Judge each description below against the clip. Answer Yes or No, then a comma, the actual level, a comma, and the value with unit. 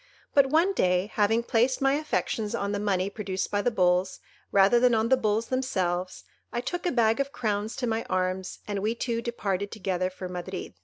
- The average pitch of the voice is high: Yes, high, 210 Hz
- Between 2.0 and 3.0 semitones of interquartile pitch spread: No, average, 4.2 semitones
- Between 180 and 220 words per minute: Yes, average, 200 wpm